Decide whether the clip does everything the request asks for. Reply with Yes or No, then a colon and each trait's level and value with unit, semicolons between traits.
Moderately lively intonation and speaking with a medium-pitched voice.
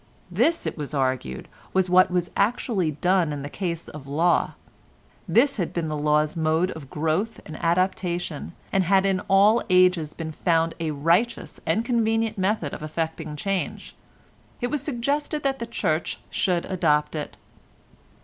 Yes: average, 4.5 semitones; medium, 175 Hz